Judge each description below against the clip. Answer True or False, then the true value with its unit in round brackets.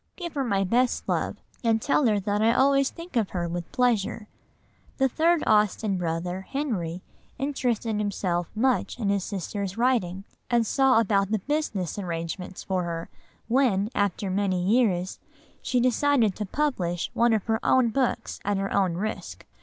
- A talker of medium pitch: False (210 Hz)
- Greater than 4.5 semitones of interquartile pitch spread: True (5.0 semitones)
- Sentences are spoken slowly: False (160 wpm)